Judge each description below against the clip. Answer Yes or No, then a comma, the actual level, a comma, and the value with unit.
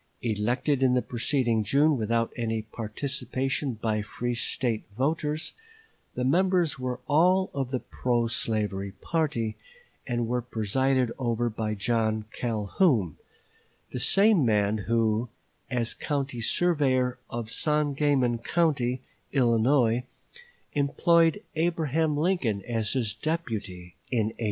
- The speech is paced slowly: Yes, slow, 115 wpm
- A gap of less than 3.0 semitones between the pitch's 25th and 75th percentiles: No, average, 4.5 semitones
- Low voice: Yes, low, 125 Hz